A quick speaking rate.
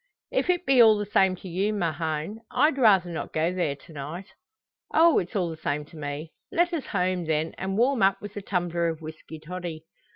Yes: fast, 215 wpm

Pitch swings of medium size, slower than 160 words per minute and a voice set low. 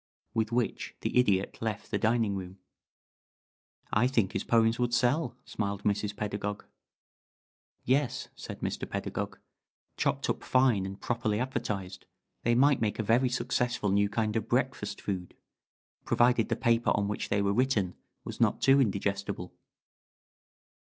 Yes: average, 3.3 semitones; average, 145 wpm; low, 110 Hz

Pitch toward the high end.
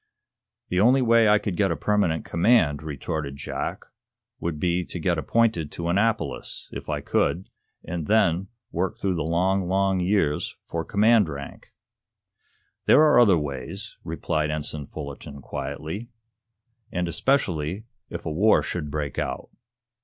No: very low, 90 Hz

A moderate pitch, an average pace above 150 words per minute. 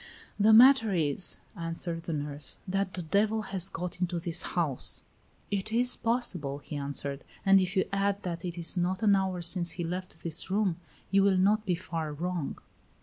Yes: medium, 180 Hz; average, 185 wpm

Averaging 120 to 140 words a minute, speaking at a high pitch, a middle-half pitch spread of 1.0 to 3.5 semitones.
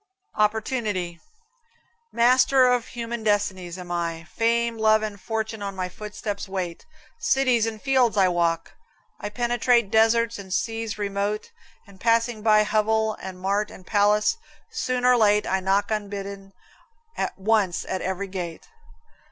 Yes: slow, 135 wpm; high, 210 Hz; average, 3.0 semitones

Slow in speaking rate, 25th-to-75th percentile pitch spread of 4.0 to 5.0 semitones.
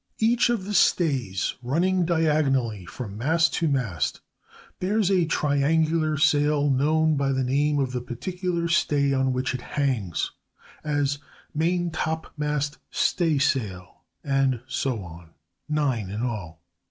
Yes: slow, 120 wpm; average, 4.3 semitones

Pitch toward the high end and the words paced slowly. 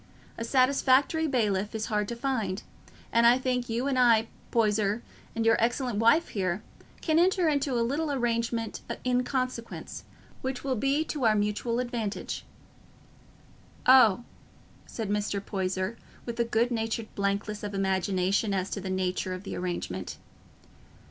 No: high, 230 Hz; average, 150 wpm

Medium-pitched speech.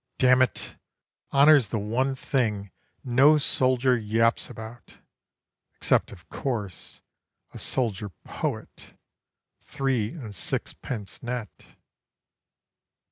No: low, 120 Hz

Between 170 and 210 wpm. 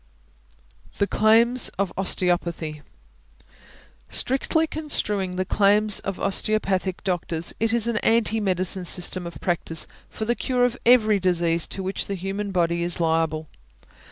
No: slow, 135 wpm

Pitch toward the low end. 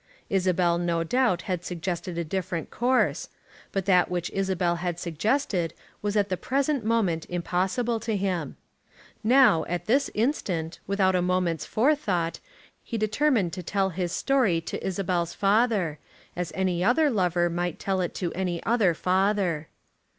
No: medium, 185 Hz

